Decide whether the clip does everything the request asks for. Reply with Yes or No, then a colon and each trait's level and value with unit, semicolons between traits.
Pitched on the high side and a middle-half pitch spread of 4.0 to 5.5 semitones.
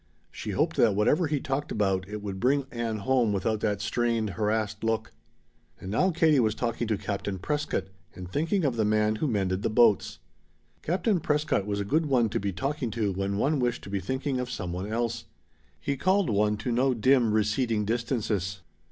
No: low, 110 Hz; average, 4.5 semitones